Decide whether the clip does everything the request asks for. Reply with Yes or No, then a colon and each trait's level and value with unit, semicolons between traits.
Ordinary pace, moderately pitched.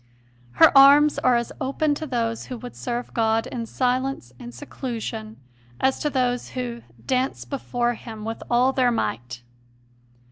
No: average, 150 wpm; high, 245 Hz